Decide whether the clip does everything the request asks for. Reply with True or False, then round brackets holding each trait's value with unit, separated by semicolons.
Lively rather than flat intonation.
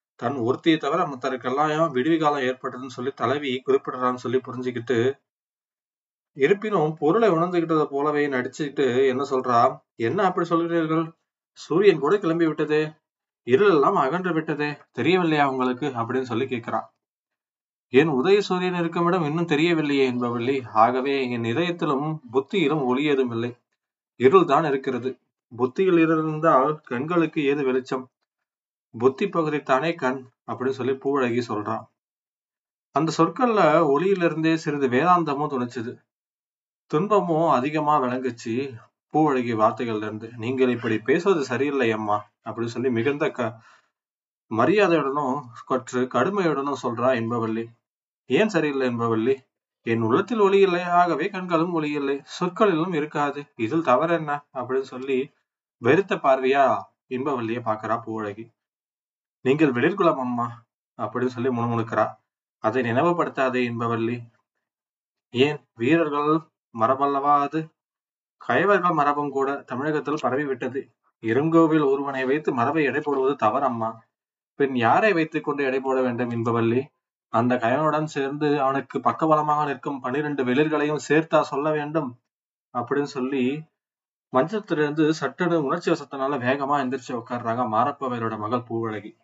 False (4.0 semitones)